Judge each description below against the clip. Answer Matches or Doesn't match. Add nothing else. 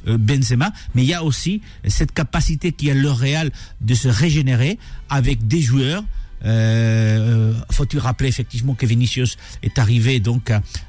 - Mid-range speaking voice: Doesn't match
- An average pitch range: Matches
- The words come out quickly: Doesn't match